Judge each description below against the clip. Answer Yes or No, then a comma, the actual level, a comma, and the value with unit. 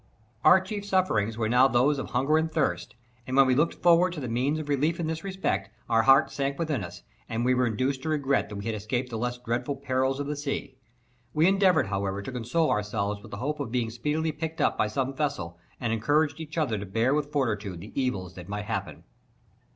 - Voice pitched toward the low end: Yes, low, 130 Hz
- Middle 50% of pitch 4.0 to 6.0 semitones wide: Yes, average, 5.3 semitones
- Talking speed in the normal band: No, fast, 230 wpm